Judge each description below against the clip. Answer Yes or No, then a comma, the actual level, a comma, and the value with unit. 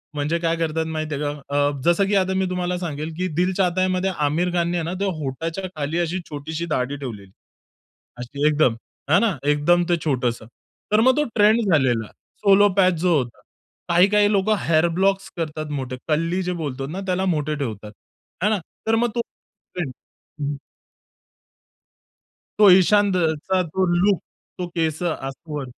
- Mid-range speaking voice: Yes, medium, 165 Hz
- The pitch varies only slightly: No, average, 4.3 semitones